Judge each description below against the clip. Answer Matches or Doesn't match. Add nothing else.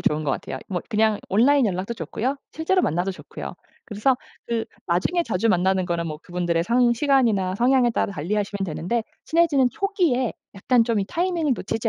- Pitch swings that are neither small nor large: Doesn't match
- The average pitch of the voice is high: Matches